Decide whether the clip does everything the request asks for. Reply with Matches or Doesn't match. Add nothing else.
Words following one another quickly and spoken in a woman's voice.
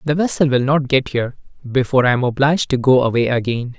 Doesn't match